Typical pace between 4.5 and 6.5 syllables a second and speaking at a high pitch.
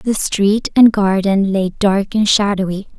No: 3.9 syllables/s; high, 200 Hz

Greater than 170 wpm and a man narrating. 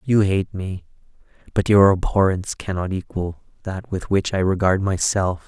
No: average, 155 wpm; male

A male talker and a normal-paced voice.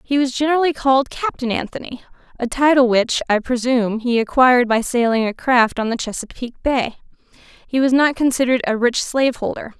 No: female; average, 165 wpm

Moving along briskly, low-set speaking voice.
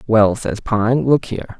No: average, 190 wpm; low, 115 Hz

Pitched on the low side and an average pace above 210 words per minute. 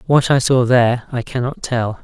No: low, 125 Hz; fast, 205 wpm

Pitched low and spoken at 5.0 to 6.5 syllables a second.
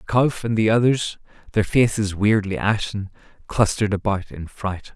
No: low, 105 Hz; 4.7 syllables/s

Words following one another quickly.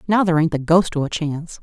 Yes: fast, 295 wpm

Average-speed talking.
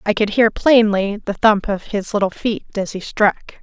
No: fast, 215 wpm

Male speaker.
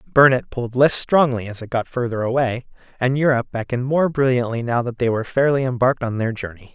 Yes: male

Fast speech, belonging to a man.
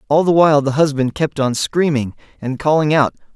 No: average, 195 wpm; male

